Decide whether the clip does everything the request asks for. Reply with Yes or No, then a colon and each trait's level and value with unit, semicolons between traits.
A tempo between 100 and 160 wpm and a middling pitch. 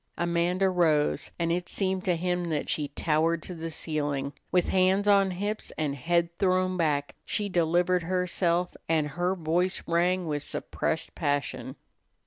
Yes: average, 150 wpm; medium, 175 Hz